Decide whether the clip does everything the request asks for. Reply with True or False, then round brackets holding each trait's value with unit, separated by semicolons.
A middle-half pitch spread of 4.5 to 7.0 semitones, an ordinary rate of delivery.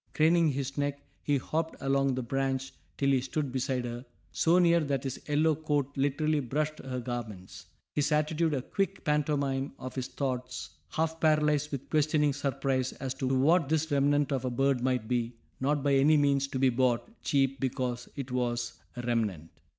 False (2.8 semitones; 180 wpm)